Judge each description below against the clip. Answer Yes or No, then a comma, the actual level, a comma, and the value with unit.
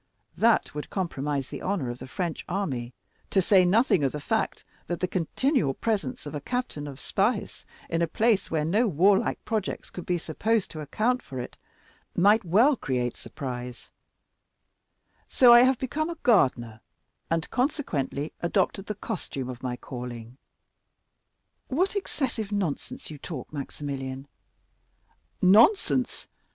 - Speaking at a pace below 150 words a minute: Yes, average, 140 wpm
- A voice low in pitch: No, medium, 175 Hz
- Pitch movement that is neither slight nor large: No, wide, 8.3 semitones